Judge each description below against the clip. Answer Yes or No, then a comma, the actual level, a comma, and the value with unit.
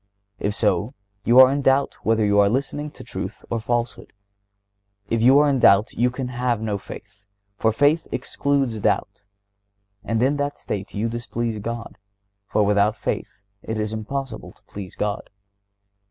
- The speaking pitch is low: Yes, low, 115 Hz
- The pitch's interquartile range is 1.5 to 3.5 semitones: No, average, 4.0 semitones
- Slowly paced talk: No, average, 165 wpm